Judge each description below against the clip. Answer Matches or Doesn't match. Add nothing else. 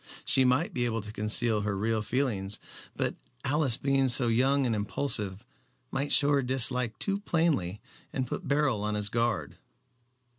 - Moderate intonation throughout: Matches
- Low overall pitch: Matches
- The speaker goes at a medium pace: Matches